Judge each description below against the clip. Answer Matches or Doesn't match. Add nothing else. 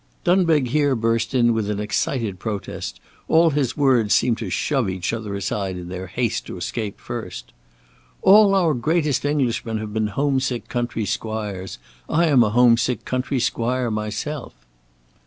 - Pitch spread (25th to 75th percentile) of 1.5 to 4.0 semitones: Doesn't match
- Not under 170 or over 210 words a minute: Doesn't match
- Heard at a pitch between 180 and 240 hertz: Doesn't match